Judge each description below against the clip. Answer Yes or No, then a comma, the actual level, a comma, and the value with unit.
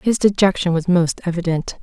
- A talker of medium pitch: Yes, medium, 180 Hz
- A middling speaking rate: Yes, average, 165 wpm